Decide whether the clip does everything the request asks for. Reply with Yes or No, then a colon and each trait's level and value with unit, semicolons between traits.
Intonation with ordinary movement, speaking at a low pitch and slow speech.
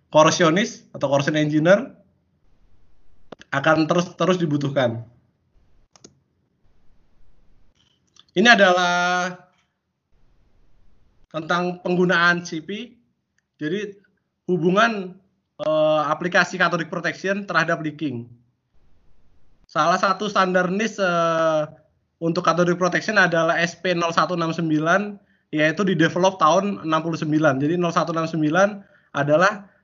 No: average, 3.4 semitones; medium, 170 Hz; slow, 75 wpm